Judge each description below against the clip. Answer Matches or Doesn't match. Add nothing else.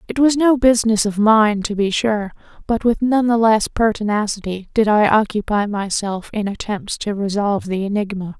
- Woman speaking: Matches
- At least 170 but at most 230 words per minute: Matches